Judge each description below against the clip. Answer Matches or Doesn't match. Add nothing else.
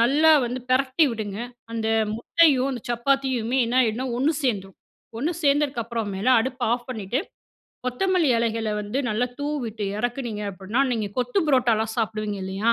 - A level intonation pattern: Doesn't match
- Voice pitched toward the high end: Matches